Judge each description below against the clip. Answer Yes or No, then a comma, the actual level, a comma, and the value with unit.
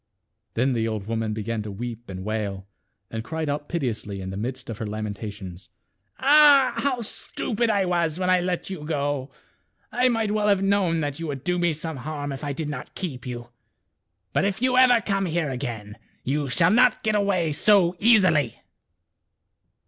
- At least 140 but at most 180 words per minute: No, average, 195 wpm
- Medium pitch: Yes, medium, 150 Hz